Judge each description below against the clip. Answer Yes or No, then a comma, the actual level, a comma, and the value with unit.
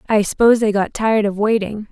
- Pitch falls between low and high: No, high, 210 Hz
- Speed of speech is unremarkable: No, fast, 220 wpm